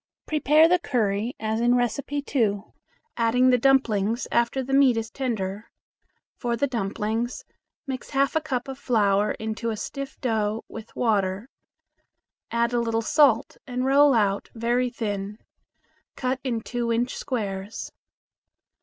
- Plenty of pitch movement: No, average, 3.2 semitones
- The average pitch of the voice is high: Yes, high, 235 Hz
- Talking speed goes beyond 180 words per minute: No, average, 140 wpm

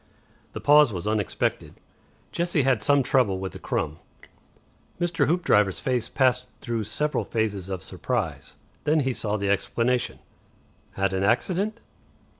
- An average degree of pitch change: No, wide, 6.3 semitones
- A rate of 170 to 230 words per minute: No, slow, 135 wpm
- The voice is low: Yes, low, 120 Hz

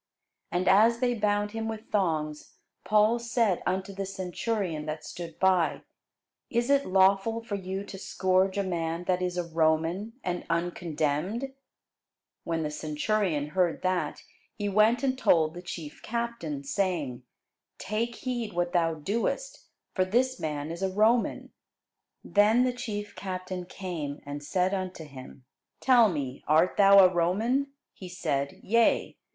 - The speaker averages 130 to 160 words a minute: Yes, average, 145 wpm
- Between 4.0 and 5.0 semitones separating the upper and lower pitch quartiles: Yes, average, 4.6 semitones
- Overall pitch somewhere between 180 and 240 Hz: Yes, medium, 185 Hz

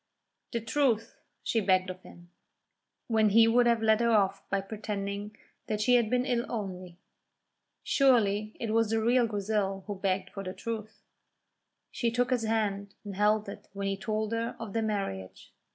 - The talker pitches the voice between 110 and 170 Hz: No, high, 215 Hz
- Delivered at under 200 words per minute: Yes, average, 175 wpm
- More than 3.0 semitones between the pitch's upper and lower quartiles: No, narrow, 2.5 semitones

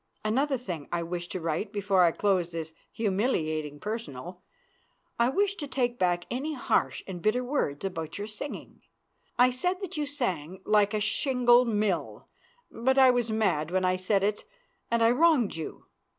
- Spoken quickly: No, average, 170 wpm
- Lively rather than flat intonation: Yes, wide, 5.9 semitones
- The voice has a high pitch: Yes, high, 210 Hz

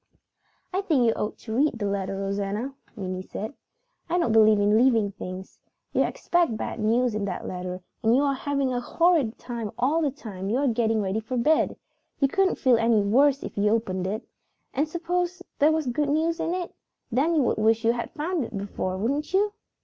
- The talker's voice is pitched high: Yes, high, 235 Hz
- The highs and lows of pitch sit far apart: Yes, wide, 6.0 semitones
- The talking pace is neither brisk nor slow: No, fast, 210 wpm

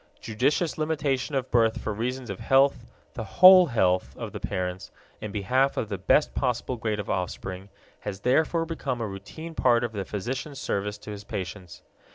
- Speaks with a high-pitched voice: No, low, 115 Hz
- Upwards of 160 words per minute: Yes, average, 180 wpm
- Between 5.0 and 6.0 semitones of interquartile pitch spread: Yes, average, 5.3 semitones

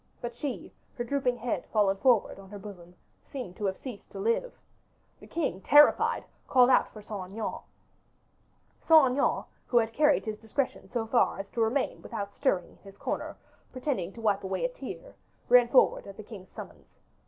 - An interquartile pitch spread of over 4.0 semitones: Yes, average, 4.7 semitones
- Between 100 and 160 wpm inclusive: No, average, 185 wpm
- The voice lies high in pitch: Yes, high, 230 Hz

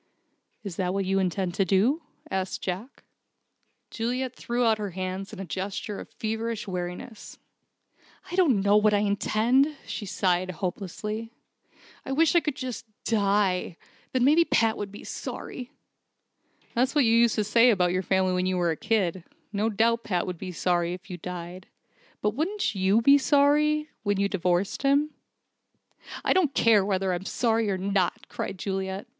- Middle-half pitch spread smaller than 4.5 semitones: Yes, average, 4.1 semitones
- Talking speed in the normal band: Yes, average, 170 wpm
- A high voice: Yes, high, 205 Hz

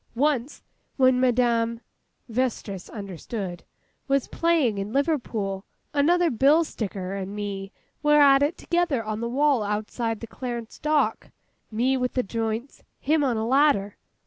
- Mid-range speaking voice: No, high, 240 Hz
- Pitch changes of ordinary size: Yes, average, 4.9 semitones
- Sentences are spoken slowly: Yes, slow, 130 wpm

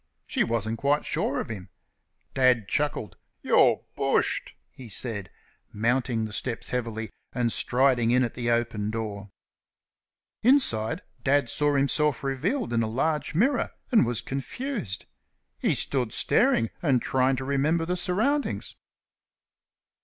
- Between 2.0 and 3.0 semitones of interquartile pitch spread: No, average, 4.3 semitones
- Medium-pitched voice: No, low, 125 Hz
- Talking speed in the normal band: No, slow, 130 wpm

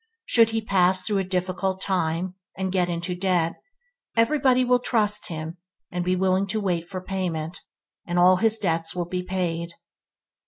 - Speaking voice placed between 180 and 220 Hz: Yes, medium, 185 Hz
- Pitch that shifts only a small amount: Yes, narrow, 2.2 semitones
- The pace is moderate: Yes, average, 165 wpm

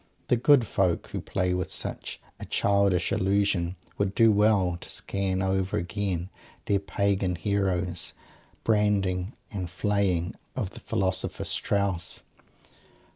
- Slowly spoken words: Yes, slow, 125 wpm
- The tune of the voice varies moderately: No, narrow, 1.9 semitones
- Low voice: Yes, very low, 95 Hz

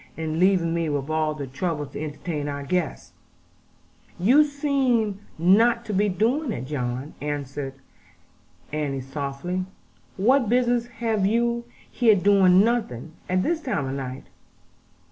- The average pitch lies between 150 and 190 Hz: Yes, medium, 185 Hz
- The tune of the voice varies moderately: No, wide, 8.0 semitones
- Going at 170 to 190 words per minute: No, average, 145 wpm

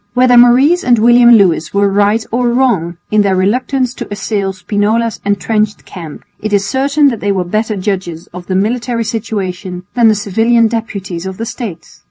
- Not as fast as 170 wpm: No, average, 180 wpm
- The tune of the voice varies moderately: Yes, average, 3.7 semitones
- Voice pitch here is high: Yes, high, 215 Hz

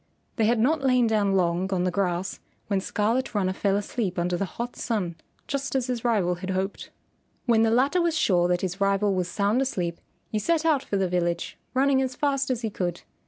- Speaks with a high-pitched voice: Yes, high, 205 Hz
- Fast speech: Yes, fast, 210 wpm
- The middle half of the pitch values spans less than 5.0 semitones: No, wide, 5.4 semitones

